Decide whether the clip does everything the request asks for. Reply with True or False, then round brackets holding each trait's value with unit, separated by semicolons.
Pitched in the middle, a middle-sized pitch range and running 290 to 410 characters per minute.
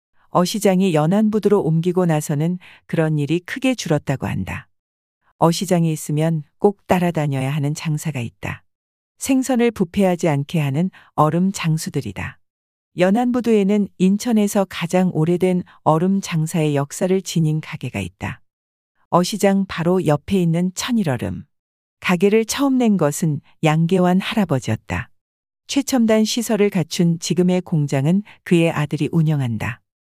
True (170 Hz; 4.8 semitones; 295 characters per minute)